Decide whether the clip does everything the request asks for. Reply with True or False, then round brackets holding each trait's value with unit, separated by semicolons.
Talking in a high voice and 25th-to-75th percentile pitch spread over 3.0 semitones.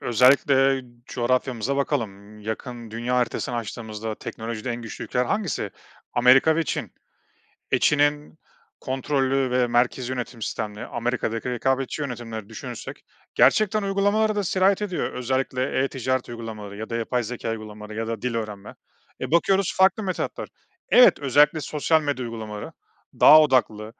False (125 Hz; 4.2 semitones)